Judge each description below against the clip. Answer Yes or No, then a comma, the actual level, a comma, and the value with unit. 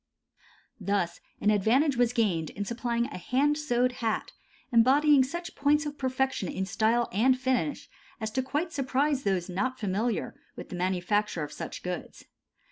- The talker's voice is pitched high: Yes, high, 240 Hz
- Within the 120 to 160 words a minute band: Yes, average, 155 wpm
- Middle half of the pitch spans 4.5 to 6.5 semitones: Yes, average, 4.9 semitones